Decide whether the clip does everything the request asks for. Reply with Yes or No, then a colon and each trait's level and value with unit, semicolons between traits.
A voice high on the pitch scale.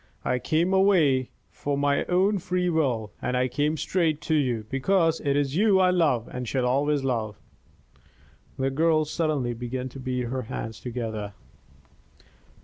No: medium, 140 Hz